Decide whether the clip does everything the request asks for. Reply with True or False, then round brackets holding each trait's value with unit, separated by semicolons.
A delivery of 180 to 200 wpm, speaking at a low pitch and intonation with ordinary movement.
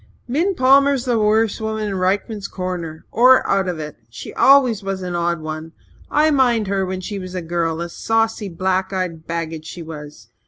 False (190 wpm; 190 Hz; 4.9 semitones)